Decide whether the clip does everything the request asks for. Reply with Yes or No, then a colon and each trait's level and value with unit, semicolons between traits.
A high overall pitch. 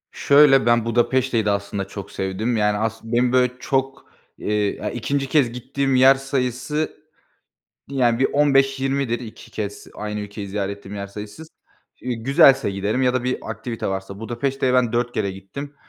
No: low, 120 Hz